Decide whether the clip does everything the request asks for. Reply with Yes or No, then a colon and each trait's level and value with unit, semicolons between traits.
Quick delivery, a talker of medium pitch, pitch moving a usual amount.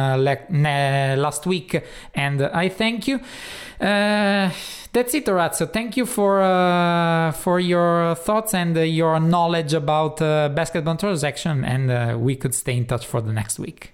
Yes: fast, 175 wpm; medium, 165 Hz; average, 5.0 semitones